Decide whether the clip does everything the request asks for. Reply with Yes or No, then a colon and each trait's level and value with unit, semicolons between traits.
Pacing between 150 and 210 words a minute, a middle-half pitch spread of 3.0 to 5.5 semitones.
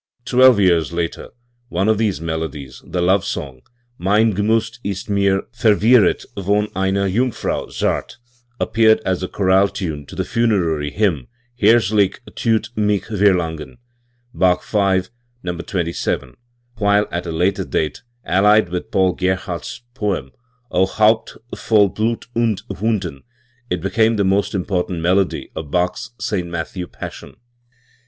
No: slow, 135 wpm; average, 3.4 semitones